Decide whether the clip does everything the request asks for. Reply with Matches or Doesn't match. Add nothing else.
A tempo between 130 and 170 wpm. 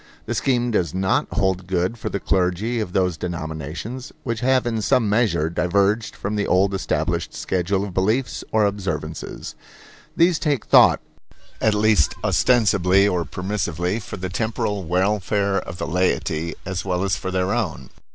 Matches